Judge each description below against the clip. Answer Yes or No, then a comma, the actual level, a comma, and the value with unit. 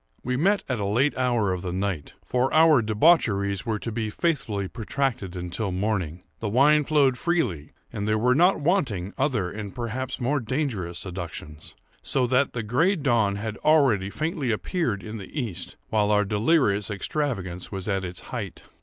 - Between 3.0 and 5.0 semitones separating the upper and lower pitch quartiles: No, wide, 5.5 semitones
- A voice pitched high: No, low, 110 Hz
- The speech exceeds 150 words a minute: Yes, average, 170 wpm